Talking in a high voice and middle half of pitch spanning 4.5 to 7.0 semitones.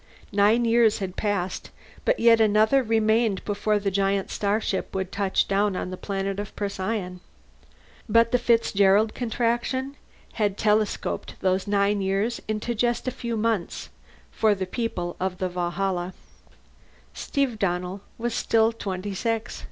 No: high, 205 Hz; average, 3.0 semitones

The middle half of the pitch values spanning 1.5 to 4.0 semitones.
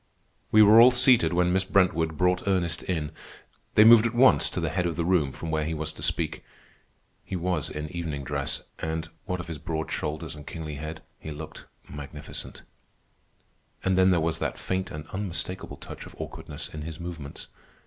Yes: average, 3.1 semitones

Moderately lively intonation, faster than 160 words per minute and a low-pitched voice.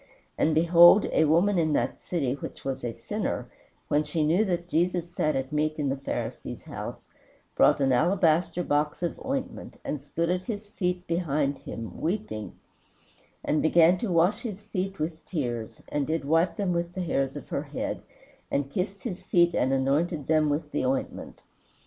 No: average, 3.7 semitones; average, 180 wpm; medium, 165 Hz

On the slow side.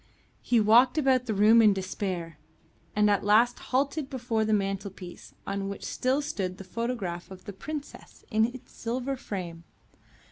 No: average, 155 wpm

